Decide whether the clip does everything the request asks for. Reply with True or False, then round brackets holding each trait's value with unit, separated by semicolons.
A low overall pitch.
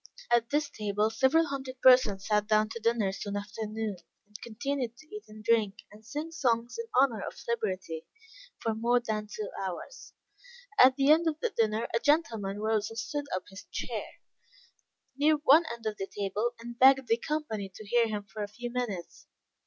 False (230 Hz)